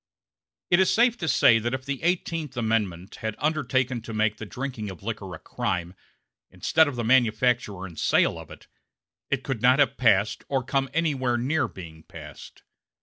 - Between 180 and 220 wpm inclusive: Yes, average, 185 wpm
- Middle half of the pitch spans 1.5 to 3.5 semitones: No, average, 4.6 semitones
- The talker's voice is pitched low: Yes, low, 125 Hz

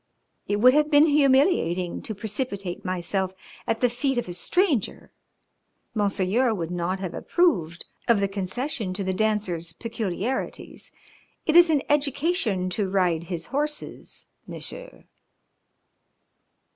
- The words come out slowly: Yes, slow, 125 wpm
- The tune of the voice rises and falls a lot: Yes, wide, 7.1 semitones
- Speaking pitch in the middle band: No, high, 210 Hz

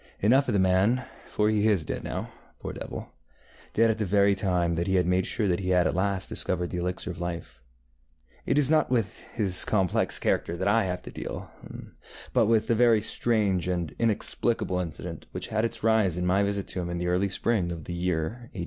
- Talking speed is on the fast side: Yes, fast, 220 wpm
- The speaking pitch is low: Yes, very low, 95 Hz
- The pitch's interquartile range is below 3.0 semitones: No, average, 3.4 semitones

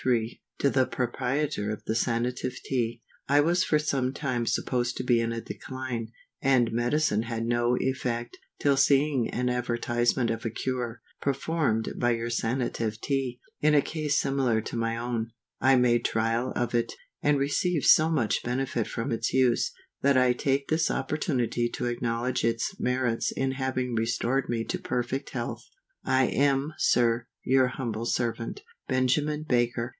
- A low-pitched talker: Yes, low, 125 Hz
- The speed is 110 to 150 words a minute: No, average, 160 wpm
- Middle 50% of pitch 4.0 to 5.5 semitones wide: No, narrow, 2.4 semitones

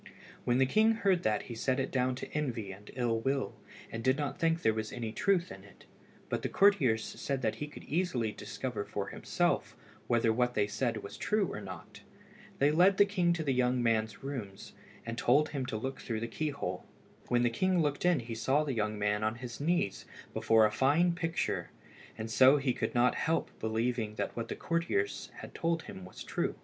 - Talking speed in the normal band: No, fast, 210 wpm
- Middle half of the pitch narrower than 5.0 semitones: No, wide, 5.4 semitones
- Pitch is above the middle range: No, low, 125 Hz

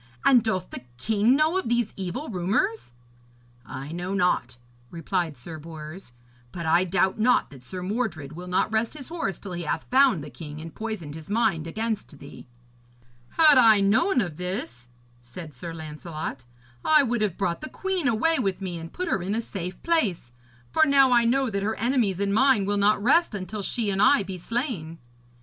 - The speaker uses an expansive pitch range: Yes, wide, 6.1 semitones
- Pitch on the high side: Yes, high, 195 Hz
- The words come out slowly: No, average, 190 wpm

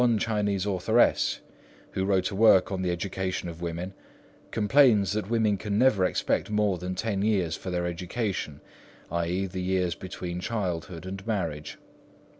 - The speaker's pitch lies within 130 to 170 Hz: No, very low, 95 Hz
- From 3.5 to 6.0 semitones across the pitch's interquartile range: No, average, 2.9 semitones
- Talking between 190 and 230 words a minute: No, average, 155 wpm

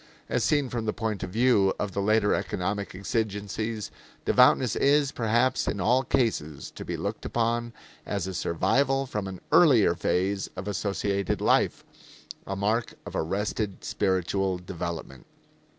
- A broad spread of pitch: No, average, 3.5 semitones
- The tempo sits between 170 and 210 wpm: No, average, 145 wpm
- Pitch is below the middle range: Yes, low, 105 Hz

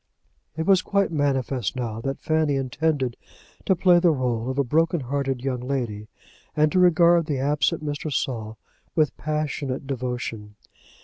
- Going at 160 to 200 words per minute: No, average, 150 wpm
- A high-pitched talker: No, medium, 140 Hz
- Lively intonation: No, average, 3.8 semitones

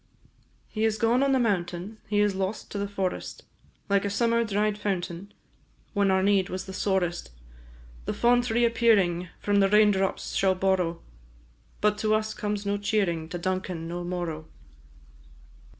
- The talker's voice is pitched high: Yes, high, 200 Hz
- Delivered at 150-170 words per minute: Yes, average, 165 wpm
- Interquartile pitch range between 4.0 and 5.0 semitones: No, narrow, 2.6 semitones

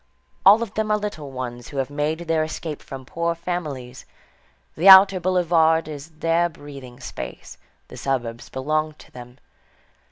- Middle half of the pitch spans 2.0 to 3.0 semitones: No, average, 4.4 semitones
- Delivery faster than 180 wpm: No, average, 155 wpm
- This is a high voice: No, medium, 155 Hz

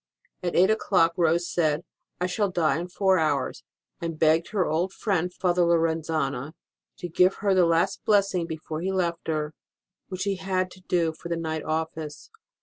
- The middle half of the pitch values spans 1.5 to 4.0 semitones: Yes, narrow, 2.5 semitones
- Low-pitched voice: No, medium, 170 Hz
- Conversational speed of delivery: Yes, average, 180 wpm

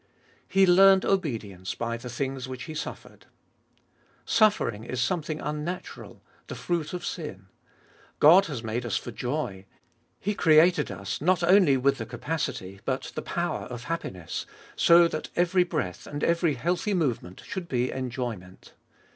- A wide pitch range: Yes, wide, 6.5 semitones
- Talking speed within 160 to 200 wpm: No, average, 145 wpm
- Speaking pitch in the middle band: Yes, medium, 150 Hz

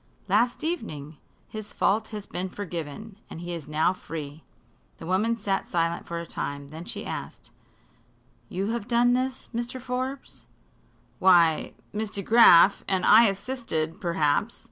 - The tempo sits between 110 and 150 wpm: Yes, average, 145 wpm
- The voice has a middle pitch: No, high, 195 Hz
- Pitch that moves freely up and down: Yes, wide, 5.7 semitones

